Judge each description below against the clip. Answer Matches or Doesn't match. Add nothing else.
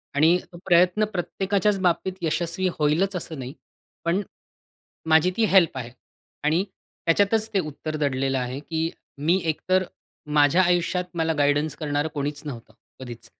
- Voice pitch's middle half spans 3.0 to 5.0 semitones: Matches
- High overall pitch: Doesn't match